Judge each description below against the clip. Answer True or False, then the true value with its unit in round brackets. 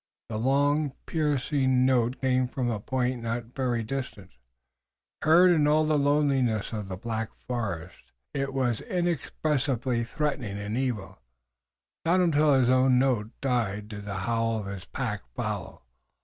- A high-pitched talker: False (125 Hz)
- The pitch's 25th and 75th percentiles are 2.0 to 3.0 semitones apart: False (4.0 semitones)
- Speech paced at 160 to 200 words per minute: False (150 wpm)